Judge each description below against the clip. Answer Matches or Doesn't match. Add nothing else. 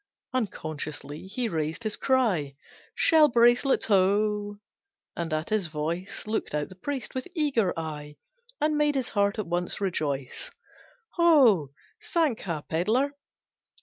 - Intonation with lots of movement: Matches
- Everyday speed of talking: Doesn't match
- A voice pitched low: Doesn't match